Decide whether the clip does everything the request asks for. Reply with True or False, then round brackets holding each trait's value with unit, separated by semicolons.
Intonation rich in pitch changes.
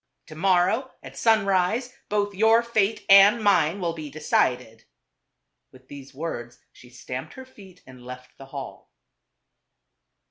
True (7.8 semitones)